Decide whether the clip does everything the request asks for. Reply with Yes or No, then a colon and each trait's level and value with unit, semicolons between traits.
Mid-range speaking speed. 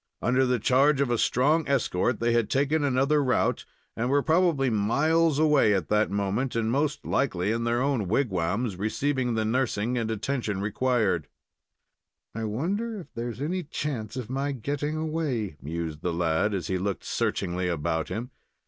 Yes: average, 170 wpm